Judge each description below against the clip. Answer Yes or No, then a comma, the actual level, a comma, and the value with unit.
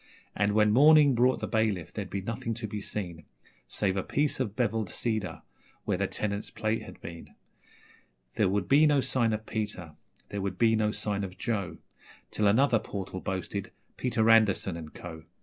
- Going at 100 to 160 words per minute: No, average, 180 wpm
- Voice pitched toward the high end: No, low, 105 Hz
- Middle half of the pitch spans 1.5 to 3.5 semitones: Yes, average, 2.9 semitones